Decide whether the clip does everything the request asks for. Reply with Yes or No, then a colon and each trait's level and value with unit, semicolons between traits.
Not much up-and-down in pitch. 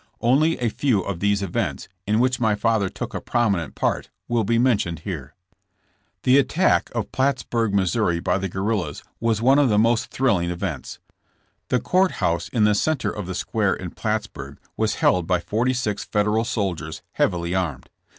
No: average, 4.4 semitones